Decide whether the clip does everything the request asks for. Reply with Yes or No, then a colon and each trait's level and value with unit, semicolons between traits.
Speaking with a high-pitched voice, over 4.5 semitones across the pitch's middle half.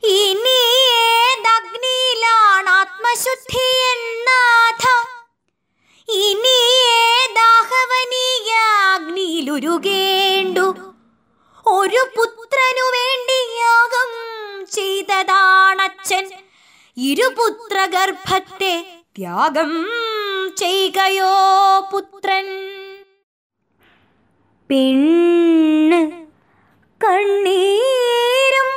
No: very high, 395 Hz; average, 3.9 semitones